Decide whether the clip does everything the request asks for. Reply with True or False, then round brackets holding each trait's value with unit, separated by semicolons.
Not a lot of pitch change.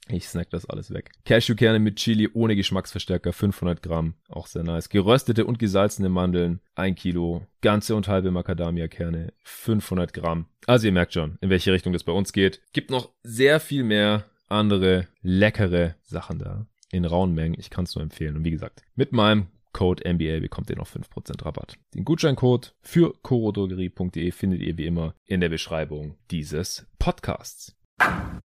False (3.8 semitones)